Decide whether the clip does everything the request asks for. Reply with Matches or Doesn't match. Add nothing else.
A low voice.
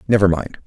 Matches